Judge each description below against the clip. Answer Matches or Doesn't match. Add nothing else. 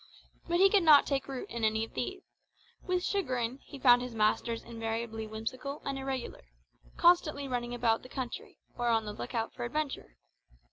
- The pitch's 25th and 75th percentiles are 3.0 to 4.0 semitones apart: Matches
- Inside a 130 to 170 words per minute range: Doesn't match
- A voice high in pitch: Matches